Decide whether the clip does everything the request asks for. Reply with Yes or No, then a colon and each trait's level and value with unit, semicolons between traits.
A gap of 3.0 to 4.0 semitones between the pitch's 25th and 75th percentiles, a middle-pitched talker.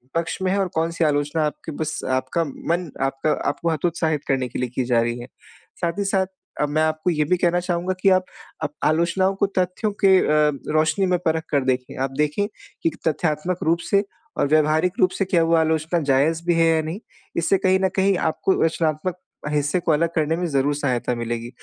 Yes: average, 3.3 semitones; medium, 160 Hz